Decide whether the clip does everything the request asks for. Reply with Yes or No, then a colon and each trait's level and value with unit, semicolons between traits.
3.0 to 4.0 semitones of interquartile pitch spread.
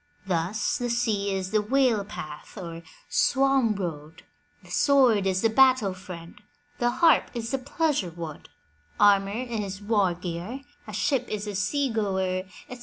No: average, 4.7 semitones